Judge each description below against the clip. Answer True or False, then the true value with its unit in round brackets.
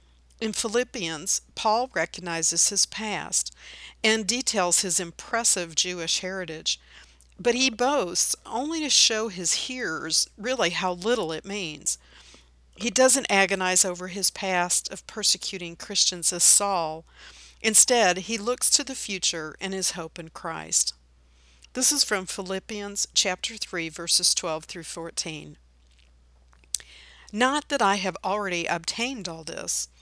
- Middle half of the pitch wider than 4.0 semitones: True (5.3 semitones)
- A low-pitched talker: False (185 Hz)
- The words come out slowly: True (130 wpm)